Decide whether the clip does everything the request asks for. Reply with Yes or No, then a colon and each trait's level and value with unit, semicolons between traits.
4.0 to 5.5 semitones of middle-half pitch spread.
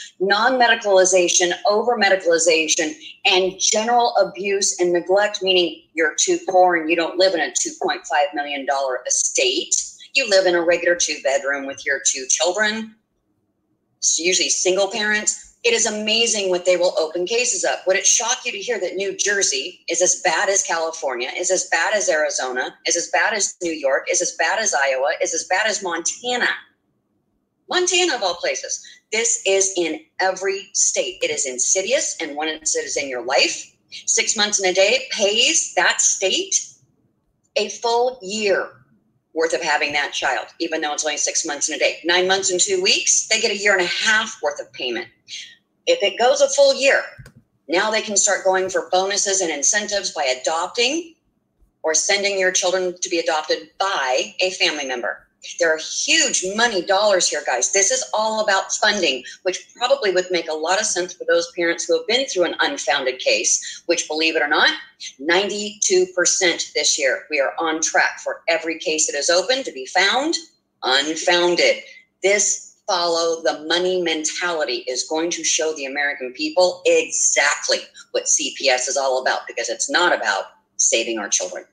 Yes: average, 4.6 semitones